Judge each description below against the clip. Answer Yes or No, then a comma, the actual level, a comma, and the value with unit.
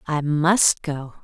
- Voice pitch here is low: No, medium, 155 Hz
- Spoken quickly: No, average, 145 wpm